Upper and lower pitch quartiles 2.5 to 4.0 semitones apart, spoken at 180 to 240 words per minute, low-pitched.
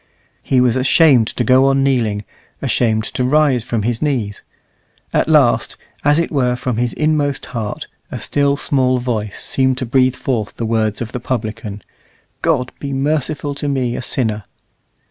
No: average, 3.3 semitones; average, 165 wpm; low, 125 Hz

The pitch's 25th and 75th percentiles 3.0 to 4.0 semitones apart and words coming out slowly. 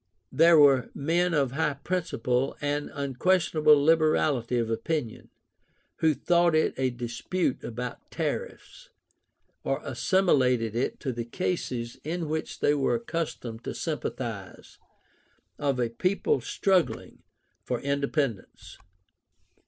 No: average, 5.1 semitones; slow, 115 wpm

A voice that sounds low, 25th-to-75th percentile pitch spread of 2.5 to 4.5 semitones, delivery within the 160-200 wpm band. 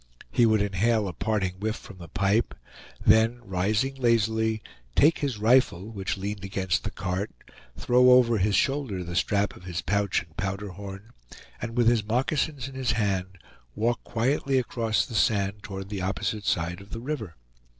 Yes: low, 105 Hz; average, 3.4 semitones; average, 170 wpm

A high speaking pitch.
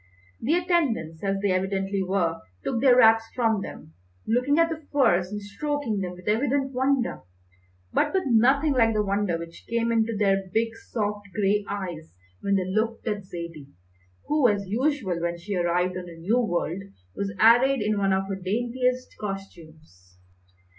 Yes: high, 205 Hz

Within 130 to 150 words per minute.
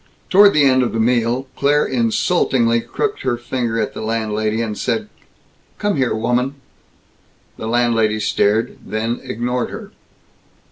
Yes: average, 140 wpm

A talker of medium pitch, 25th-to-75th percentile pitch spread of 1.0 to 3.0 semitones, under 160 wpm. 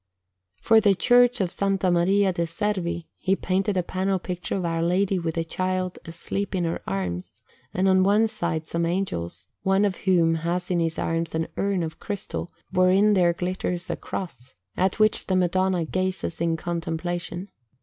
No: medium, 180 Hz; narrow, 2.4 semitones; average, 175 wpm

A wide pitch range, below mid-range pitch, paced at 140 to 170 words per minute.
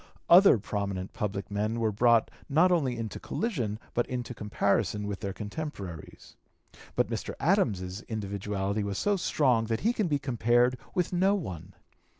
Yes: wide, 5.8 semitones; low, 110 Hz; average, 150 wpm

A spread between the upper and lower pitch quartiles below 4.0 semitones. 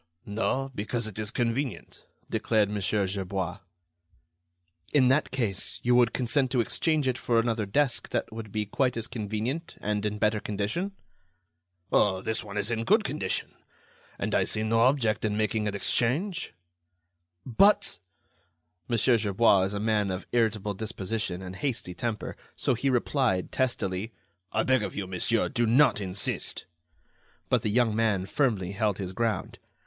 Yes: average, 3.2 semitones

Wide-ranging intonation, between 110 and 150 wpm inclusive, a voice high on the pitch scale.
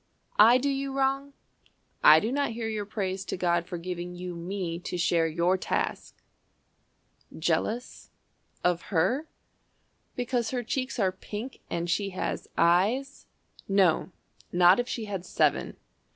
Yes: wide, 5.7 semitones; average, 140 wpm; high, 195 Hz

